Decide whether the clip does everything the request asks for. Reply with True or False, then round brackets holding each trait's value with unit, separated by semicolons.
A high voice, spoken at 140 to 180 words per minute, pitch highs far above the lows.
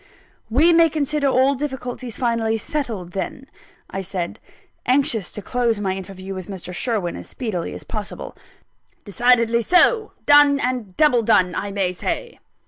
True (230 Hz; 145 wpm; 6.0 semitones)